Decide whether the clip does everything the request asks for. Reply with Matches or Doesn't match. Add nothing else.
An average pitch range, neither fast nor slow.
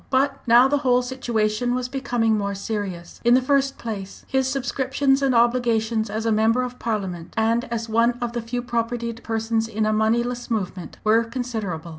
Doesn't match